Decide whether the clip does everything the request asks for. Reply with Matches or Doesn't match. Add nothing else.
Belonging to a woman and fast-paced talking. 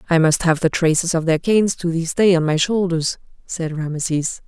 Matches